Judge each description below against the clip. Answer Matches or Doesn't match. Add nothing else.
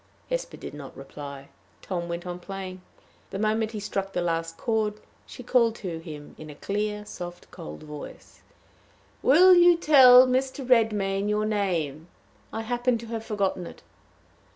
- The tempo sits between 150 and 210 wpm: Matches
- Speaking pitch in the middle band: Doesn't match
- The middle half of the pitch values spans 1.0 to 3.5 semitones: Doesn't match